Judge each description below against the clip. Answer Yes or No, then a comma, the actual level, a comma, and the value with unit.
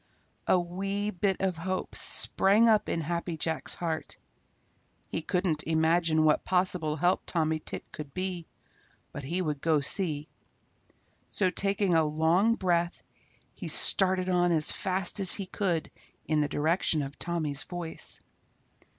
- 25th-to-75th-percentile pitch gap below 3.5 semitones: Yes, average, 3.0 semitones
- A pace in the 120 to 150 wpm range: Yes, average, 140 wpm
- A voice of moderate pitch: Yes, medium, 175 Hz